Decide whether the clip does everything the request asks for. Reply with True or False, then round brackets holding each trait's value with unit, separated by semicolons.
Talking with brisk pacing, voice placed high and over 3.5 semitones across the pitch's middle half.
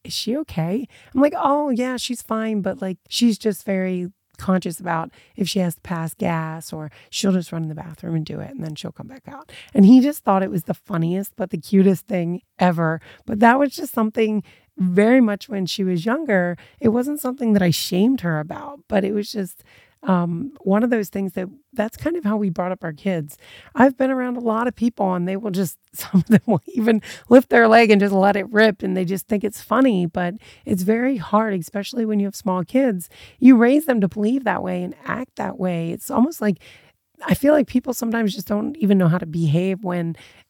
True (230 wpm; 200 Hz; 4.5 semitones)